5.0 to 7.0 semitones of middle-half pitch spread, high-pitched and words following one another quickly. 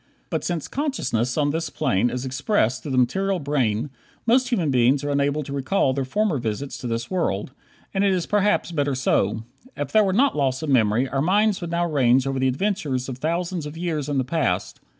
No: wide, 5.5 semitones; medium, 145 Hz; fast, 210 wpm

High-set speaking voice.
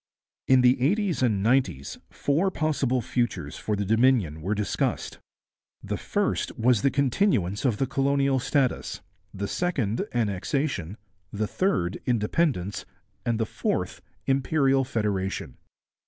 No: low, 125 Hz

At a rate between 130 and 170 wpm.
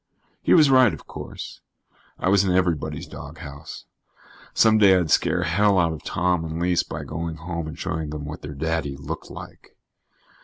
No: average, 180 wpm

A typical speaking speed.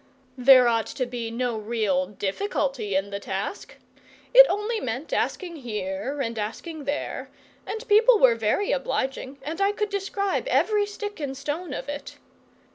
Yes: average, 155 wpm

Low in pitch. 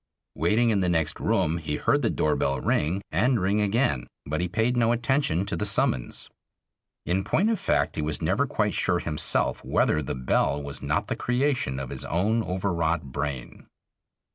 Yes: very low, 90 Hz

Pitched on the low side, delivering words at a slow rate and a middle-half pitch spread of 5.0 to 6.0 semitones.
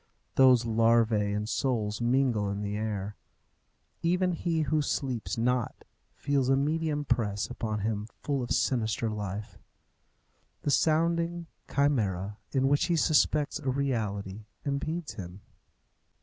Yes: low, 125 Hz; slow, 125 wpm; wide, 5.4 semitones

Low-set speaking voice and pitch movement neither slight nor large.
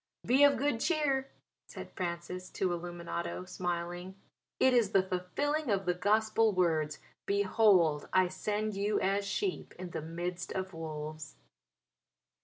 No: medium, 185 Hz; average, 3.9 semitones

